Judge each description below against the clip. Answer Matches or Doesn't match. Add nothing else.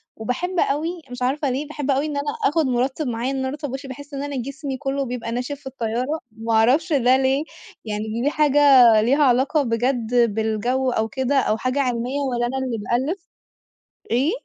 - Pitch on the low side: Doesn't match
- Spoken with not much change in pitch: Doesn't match